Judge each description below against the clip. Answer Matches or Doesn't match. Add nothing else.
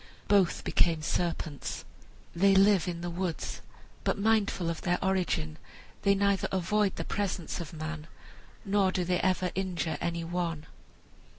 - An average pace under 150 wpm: Matches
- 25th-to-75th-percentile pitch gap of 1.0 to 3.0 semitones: Matches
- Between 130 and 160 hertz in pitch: Doesn't match